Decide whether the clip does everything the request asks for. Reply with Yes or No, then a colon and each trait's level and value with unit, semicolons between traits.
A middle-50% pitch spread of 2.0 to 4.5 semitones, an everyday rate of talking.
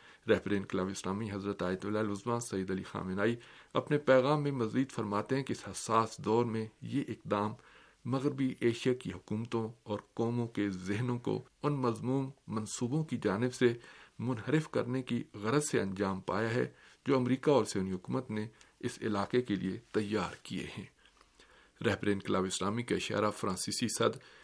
Yes: average, 3.7 semitones; average, 155 wpm